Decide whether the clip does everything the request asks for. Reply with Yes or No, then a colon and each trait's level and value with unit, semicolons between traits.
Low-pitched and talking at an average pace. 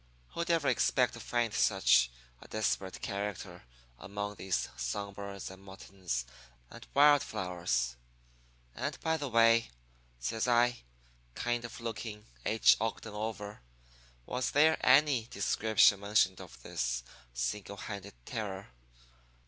No: low, 105 Hz; slow, 125 wpm